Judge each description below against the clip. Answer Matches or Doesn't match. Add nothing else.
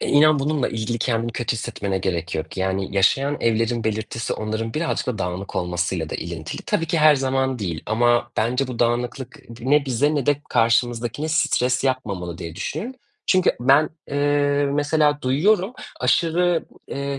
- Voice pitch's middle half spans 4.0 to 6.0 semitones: Matches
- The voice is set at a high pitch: Doesn't match